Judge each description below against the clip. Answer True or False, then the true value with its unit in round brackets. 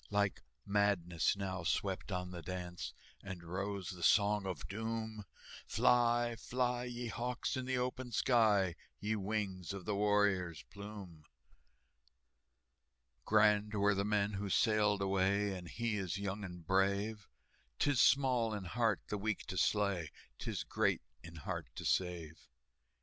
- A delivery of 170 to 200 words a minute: False (140 wpm)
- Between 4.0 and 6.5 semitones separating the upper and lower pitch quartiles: False (2.7 semitones)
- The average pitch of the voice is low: True (100 Hz)